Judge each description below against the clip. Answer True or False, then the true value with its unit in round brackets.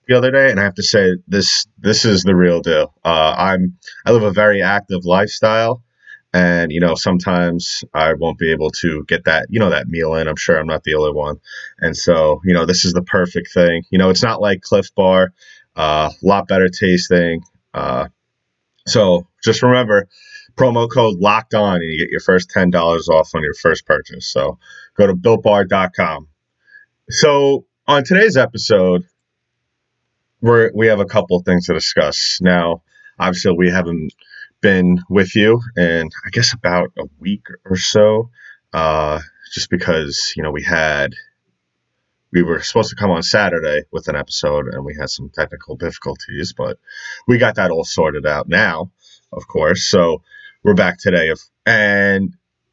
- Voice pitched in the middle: False (95 Hz)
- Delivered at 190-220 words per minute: False (180 wpm)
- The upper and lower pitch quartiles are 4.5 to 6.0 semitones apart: True (5.1 semitones)